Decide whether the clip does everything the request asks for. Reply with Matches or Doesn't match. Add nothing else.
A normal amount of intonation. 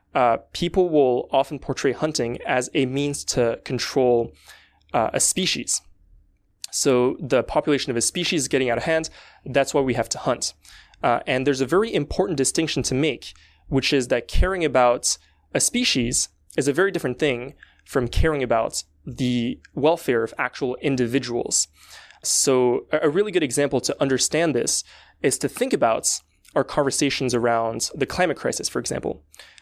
Matches